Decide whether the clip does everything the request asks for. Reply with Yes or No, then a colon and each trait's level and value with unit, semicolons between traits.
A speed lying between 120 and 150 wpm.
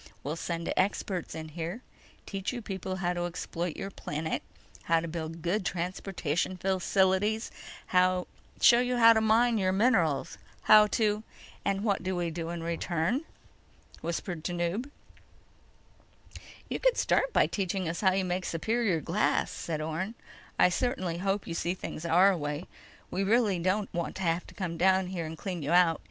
No: average, 165 wpm